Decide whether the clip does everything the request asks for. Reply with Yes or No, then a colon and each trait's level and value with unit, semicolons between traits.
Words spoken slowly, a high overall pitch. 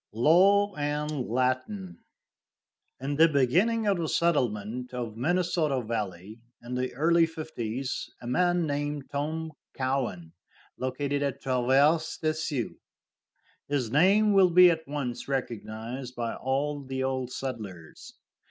No: slow, 125 wpm; medium, 140 Hz